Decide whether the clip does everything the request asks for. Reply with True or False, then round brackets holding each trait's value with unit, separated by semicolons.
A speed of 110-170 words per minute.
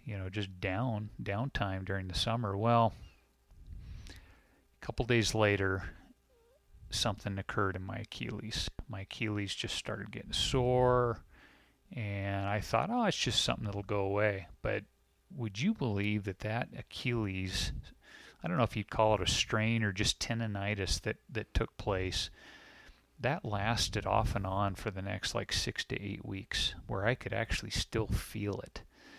True (160 wpm)